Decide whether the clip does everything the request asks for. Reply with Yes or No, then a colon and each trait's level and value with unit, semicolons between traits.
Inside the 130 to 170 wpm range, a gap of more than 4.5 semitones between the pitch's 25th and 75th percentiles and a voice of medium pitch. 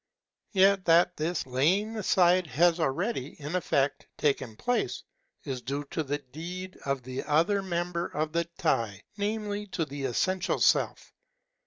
Yes: average, 145 wpm; average, 5.0 semitones; medium, 170 Hz